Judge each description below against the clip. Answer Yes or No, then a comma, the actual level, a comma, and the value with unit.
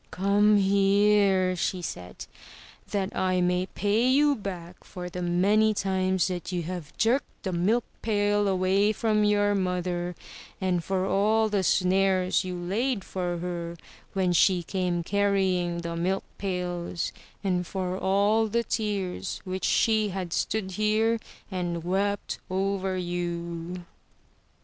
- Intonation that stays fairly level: Yes, narrow, 2.3 semitones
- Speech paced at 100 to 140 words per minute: Yes, slow, 135 wpm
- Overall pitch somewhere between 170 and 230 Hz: Yes, high, 190 Hz